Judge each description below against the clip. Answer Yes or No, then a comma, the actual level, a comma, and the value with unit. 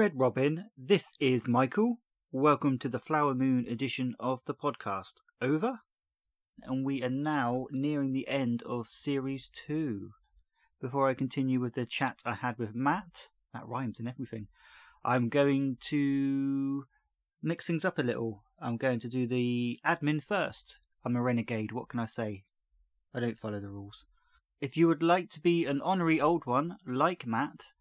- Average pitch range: Yes, average, 3.5 semitones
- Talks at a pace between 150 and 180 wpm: Yes, average, 170 wpm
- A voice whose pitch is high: No, low, 130 Hz